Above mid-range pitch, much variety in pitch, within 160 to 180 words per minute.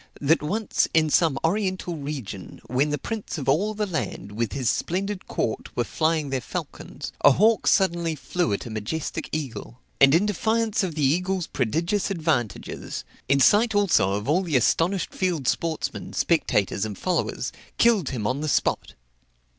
No: medium, 160 Hz; wide, 6.0 semitones; average, 165 wpm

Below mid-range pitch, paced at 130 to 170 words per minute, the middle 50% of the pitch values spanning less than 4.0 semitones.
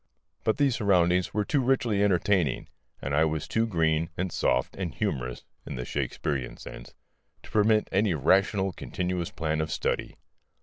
No: very low, 90 Hz; average, 160 wpm; average, 4.8 semitones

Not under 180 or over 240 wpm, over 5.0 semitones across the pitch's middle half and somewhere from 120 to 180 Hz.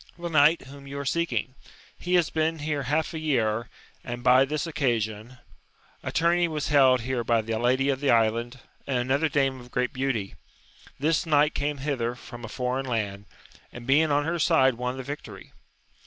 No: average, 190 wpm; average, 3.6 semitones; low, 135 Hz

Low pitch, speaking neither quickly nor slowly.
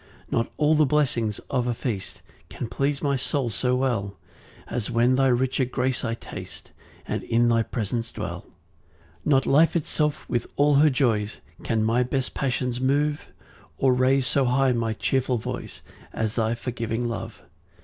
Yes: low, 125 Hz; average, 170 wpm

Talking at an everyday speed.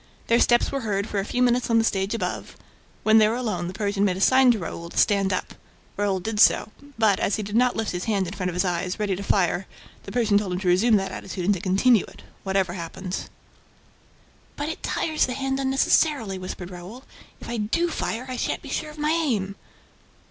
No: fast, 230 wpm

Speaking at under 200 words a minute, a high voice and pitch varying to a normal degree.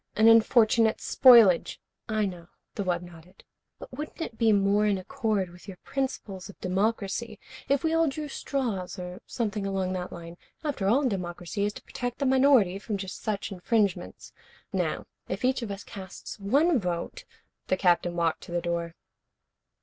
Yes: average, 175 wpm; high, 200 Hz; average, 4.5 semitones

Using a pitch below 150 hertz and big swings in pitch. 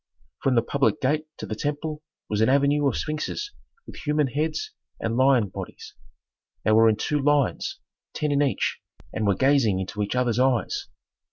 No: low, 135 Hz; average, 4.7 semitones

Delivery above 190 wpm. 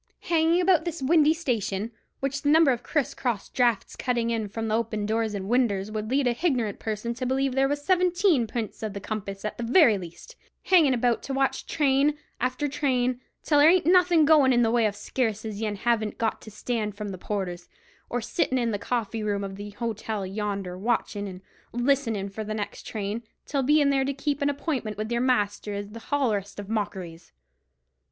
Yes: average, 200 wpm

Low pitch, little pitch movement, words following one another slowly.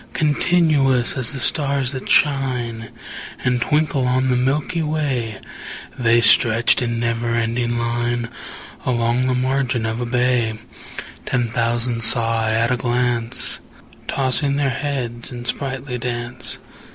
Yes: low, 125 Hz; narrow, 2.3 semitones; slow, 130 wpm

